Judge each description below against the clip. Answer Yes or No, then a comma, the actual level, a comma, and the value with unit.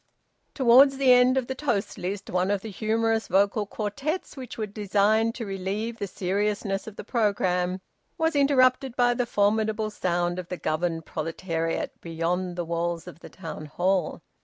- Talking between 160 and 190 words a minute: Yes, average, 165 wpm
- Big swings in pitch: No, average, 4.5 semitones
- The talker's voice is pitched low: No, high, 205 Hz